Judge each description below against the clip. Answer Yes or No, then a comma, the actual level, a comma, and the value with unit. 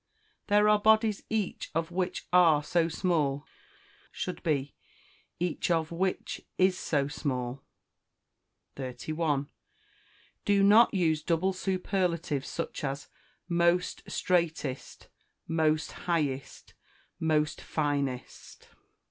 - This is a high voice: No, medium, 165 Hz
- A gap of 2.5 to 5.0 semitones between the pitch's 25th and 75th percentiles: Yes, average, 3.9 semitones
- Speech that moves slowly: Yes, slow, 95 wpm